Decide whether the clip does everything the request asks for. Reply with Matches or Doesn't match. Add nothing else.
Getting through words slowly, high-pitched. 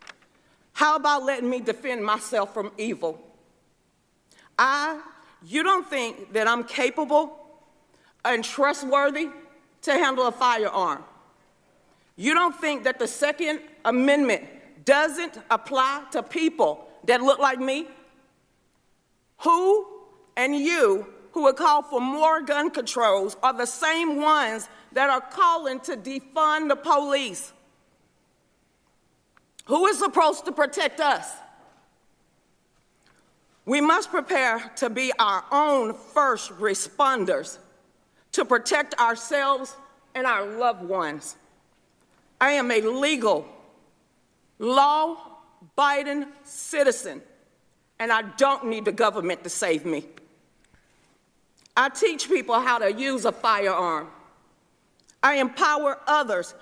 Matches